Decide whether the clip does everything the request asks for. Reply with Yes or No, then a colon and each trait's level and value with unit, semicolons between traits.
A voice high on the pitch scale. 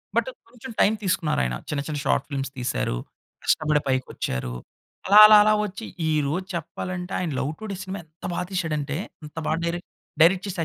No: medium, 165 Hz